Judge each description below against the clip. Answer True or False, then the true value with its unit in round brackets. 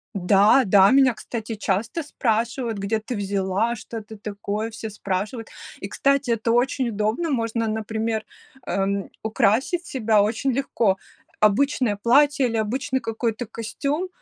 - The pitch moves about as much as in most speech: True (3.2 semitones)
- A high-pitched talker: True (225 Hz)